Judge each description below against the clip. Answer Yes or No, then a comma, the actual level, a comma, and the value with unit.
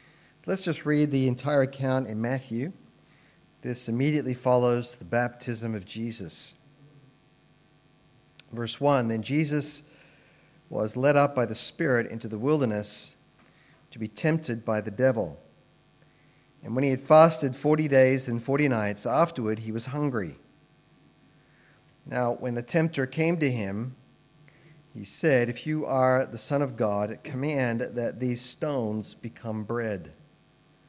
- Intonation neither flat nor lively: Yes, average, 4.2 semitones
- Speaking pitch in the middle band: No, low, 130 Hz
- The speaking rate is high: No, slow, 135 wpm